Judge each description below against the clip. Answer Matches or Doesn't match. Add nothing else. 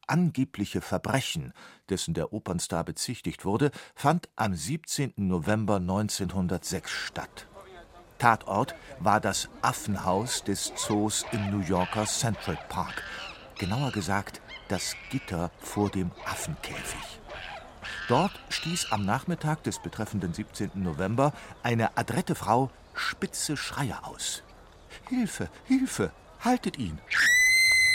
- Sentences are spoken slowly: Matches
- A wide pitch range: Matches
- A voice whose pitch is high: Doesn't match